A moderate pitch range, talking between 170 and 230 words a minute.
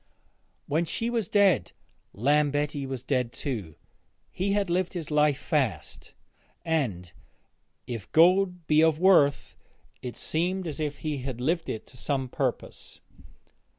No: average, 4.8 semitones; slow, 135 wpm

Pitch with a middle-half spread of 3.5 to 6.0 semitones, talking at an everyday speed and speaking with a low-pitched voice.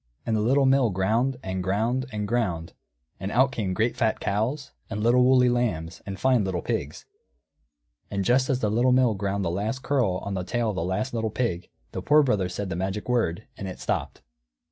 No: average, 4.6 semitones; fast, 210 wpm; low, 110 Hz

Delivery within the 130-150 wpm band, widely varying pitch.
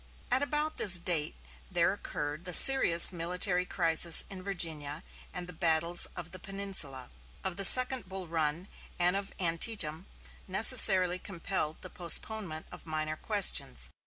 No: average, 140 wpm; average, 3.3 semitones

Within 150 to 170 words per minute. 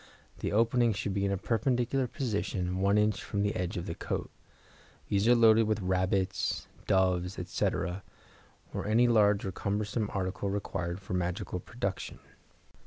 Yes: average, 155 wpm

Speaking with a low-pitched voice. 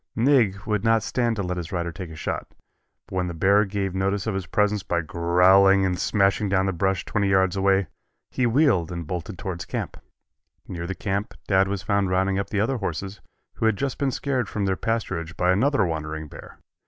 Yes: very low, 95 Hz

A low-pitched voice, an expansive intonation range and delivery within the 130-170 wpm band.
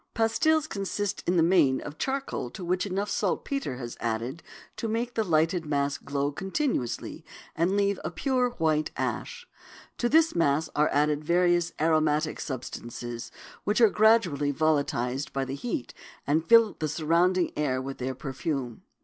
No: medium, 160 Hz; wide, 6.4 semitones; average, 155 wpm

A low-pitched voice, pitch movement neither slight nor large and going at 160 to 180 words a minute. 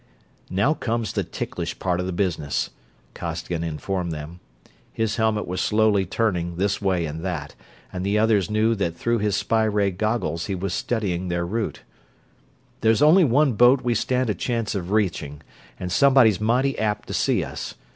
Yes: low, 100 Hz; average, 4.2 semitones; average, 175 wpm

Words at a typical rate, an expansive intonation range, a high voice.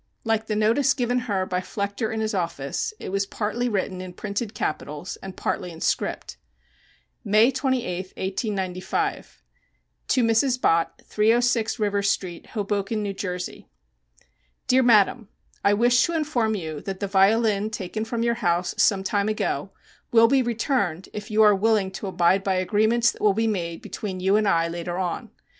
No: average, 165 wpm; average, 3.3 semitones; high, 205 Hz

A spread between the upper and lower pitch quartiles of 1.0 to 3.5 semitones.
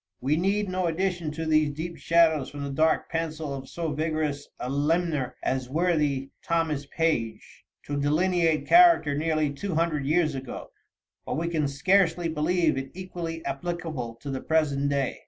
Yes: average, 3.0 semitones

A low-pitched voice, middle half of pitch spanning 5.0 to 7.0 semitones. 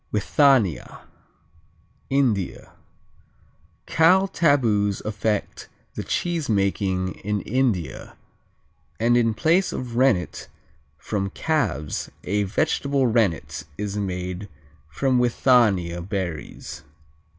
Yes: low, 105 Hz; wide, 5.6 semitones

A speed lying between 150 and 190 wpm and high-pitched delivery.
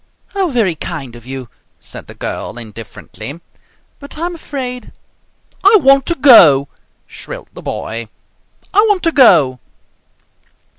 No: slow, 135 wpm; high, 235 Hz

